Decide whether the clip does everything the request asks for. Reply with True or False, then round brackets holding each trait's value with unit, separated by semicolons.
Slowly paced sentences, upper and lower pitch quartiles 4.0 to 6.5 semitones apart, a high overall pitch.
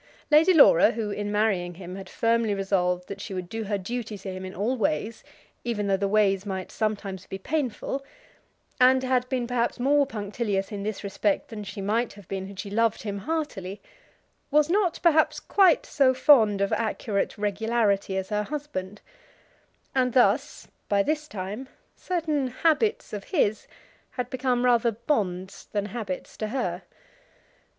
False (165 wpm; 4.5 semitones; 215 Hz)